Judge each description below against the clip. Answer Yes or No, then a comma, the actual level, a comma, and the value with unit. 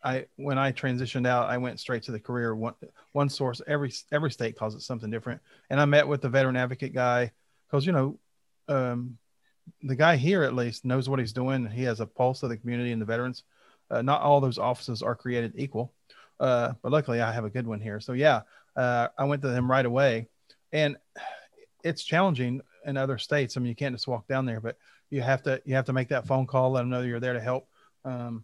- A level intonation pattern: Yes, narrow, 2.3 semitones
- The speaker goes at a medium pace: No, fast, 235 wpm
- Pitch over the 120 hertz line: Yes, low, 130 Hz